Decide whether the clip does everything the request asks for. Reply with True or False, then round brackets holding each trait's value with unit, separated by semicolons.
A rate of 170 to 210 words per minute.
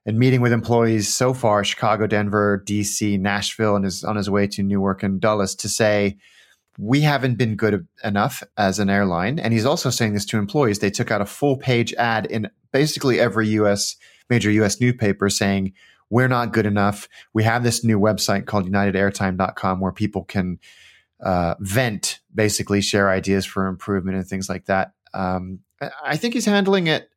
True (180 wpm)